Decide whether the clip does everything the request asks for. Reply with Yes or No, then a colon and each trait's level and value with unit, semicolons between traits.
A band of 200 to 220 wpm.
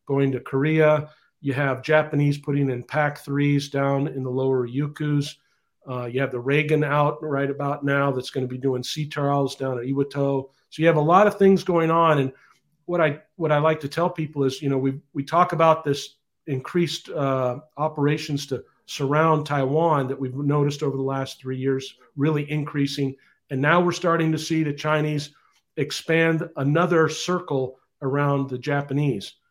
No: average, 185 wpm